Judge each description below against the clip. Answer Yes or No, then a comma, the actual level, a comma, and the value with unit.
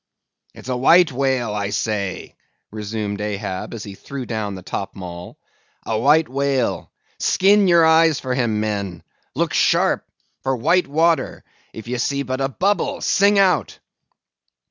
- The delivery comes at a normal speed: Yes, average, 145 wpm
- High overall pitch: No, low, 125 Hz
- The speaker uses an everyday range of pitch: No, wide, 7.4 semitones